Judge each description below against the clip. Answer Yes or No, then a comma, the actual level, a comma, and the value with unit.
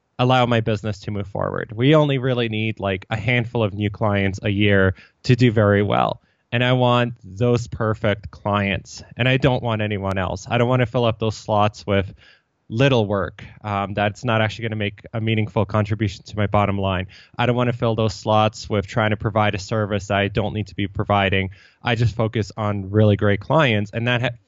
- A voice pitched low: Yes, low, 110 Hz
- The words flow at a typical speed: No, fast, 215 wpm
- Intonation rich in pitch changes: No, average, 2.7 semitones